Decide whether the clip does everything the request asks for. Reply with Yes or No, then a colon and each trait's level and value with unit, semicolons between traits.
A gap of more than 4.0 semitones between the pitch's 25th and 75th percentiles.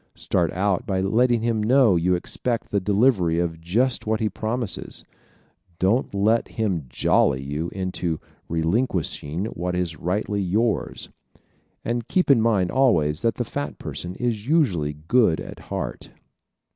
Yes: average, 5.1 semitones